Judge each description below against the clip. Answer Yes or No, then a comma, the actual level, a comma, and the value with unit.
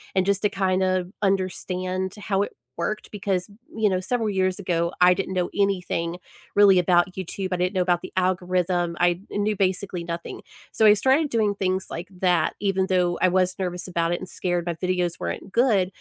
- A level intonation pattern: Yes, narrow, 1.7 semitones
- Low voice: No, medium, 185 Hz